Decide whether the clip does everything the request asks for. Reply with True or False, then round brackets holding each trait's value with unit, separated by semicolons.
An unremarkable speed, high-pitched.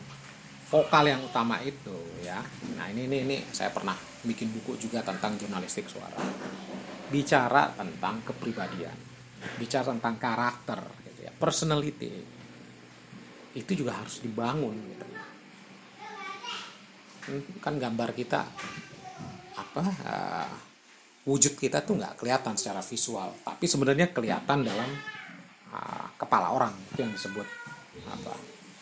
False (110 wpm; 135 Hz)